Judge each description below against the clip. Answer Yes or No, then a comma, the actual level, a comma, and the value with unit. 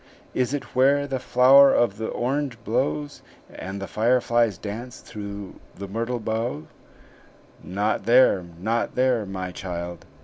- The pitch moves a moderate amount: Yes, average, 4.5 semitones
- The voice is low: Yes, low, 110 Hz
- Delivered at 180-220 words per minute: No, slow, 135 wpm